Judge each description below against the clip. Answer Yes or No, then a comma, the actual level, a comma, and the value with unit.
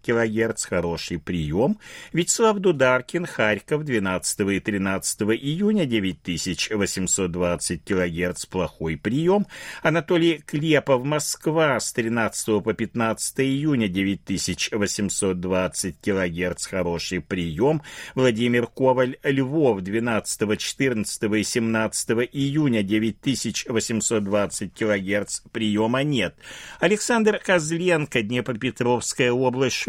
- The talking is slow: Yes, slow, 85 wpm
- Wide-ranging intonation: Yes, wide, 5.7 semitones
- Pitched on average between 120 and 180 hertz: No, low, 110 Hz